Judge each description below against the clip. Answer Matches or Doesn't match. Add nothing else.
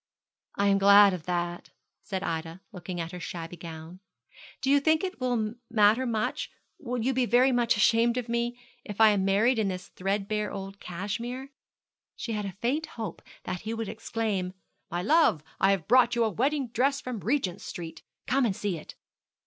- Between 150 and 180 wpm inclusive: Doesn't match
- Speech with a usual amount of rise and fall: Matches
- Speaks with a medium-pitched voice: Doesn't match